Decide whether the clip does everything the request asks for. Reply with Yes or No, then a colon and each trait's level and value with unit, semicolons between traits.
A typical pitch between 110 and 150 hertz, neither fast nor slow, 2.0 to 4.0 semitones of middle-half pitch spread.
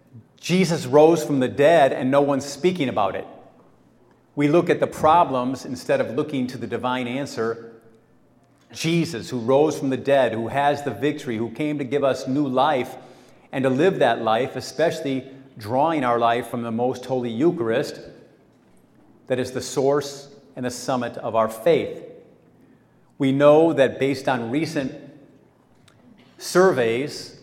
Yes: low, 135 Hz; average, 155 wpm; average, 2.8 semitones